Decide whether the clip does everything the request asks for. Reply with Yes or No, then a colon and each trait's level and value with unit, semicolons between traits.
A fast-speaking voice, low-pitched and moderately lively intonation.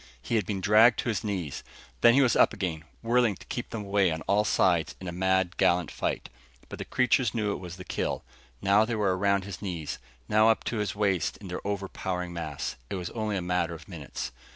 Yes: fast, 225 wpm; low, 100 Hz; average, 3.2 semitones